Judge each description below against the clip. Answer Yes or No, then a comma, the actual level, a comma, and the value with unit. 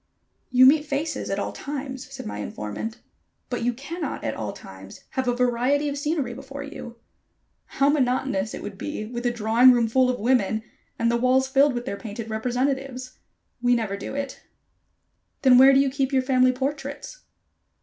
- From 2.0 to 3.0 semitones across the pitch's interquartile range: Yes, narrow, 2.6 semitones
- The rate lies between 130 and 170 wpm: No, average, 180 wpm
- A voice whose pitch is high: Yes, very high, 255 Hz